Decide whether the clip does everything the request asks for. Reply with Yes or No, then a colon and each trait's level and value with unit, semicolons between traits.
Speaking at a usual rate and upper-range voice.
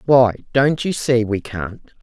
No: average, 180 wpm; low, 125 Hz